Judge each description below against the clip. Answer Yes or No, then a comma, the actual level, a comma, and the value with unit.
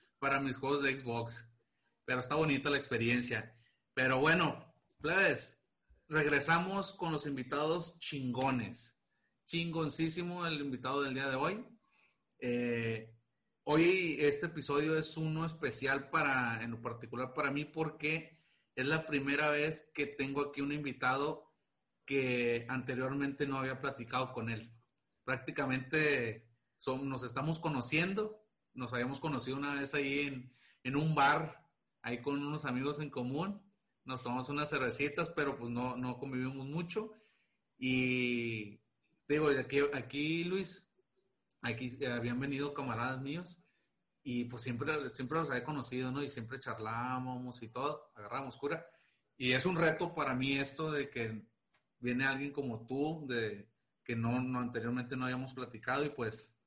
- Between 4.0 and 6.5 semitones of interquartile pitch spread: No, average, 3.5 semitones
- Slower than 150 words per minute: Yes, average, 140 wpm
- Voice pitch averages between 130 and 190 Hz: Yes, low, 135 Hz